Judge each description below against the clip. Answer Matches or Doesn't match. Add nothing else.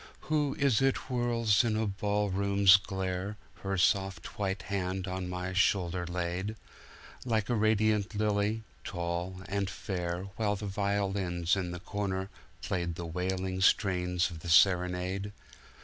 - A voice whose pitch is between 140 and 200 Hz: Doesn't match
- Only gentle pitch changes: Matches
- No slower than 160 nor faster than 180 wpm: Doesn't match